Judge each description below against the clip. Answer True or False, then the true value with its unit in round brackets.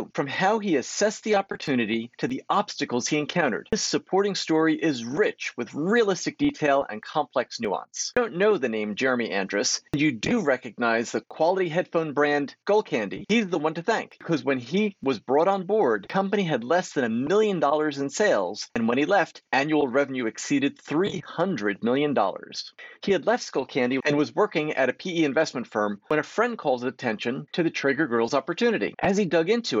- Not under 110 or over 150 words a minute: False (195 wpm)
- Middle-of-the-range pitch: True (160 Hz)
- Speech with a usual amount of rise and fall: False (6.6 semitones)